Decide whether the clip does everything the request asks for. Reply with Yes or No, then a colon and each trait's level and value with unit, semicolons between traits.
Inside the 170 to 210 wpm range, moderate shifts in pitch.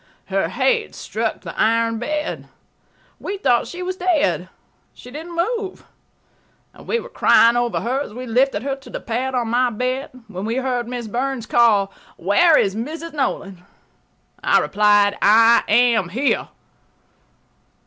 No: average, 150 wpm; average, 5.0 semitones